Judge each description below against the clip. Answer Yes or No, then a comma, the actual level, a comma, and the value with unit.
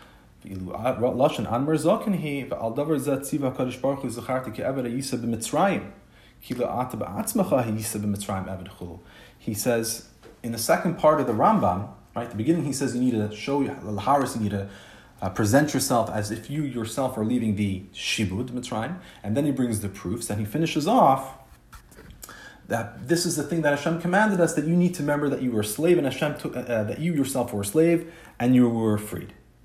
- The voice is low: Yes, low, 125 Hz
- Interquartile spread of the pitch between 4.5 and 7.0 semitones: Yes, average, 5.3 semitones